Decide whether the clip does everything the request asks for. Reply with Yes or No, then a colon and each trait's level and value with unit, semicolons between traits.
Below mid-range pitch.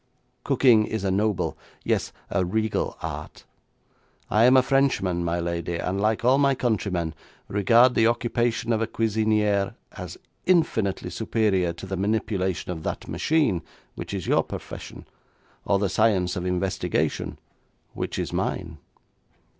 Yes: low, 105 Hz